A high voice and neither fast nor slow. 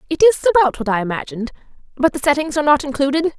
Yes: very high, 290 Hz; average, 195 wpm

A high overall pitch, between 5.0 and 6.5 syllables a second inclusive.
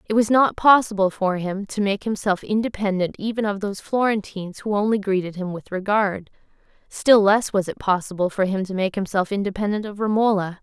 Yes: high, 200 Hz; 5.6 syllables/s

